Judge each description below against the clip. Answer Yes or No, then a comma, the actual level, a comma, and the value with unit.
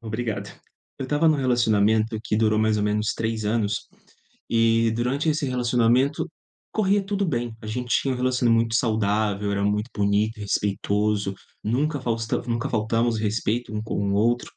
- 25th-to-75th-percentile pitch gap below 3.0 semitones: Yes, narrow, 2.5 semitones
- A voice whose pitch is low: Yes, low, 115 Hz